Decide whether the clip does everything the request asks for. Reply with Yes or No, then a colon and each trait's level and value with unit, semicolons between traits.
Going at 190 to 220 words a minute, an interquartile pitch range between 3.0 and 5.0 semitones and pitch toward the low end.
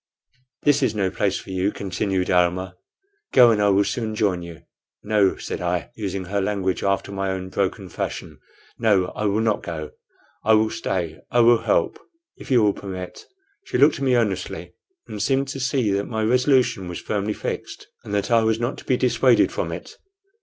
Yes: average, 195 wpm; average, 3.7 semitones; low, 100 Hz